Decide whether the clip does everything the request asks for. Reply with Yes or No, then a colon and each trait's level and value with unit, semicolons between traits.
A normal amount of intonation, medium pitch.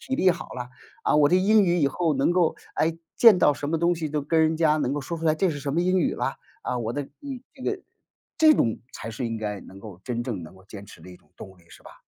No: wide, 6.7 semitones; medium, 150 Hz